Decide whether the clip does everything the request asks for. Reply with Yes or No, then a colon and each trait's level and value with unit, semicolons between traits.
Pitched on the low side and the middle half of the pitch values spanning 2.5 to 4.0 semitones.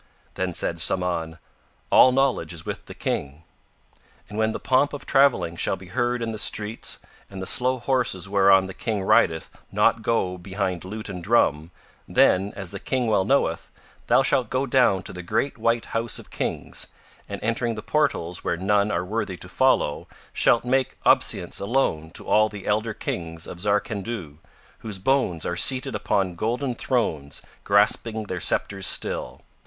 No: low, 105 Hz; average, 4.7 semitones